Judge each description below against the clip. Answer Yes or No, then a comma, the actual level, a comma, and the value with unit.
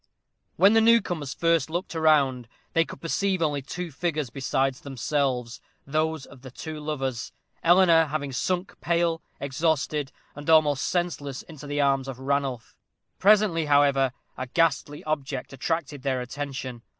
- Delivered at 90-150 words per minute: Yes, average, 140 wpm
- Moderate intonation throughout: Yes, average, 3.5 semitones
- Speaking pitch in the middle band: Yes, medium, 145 Hz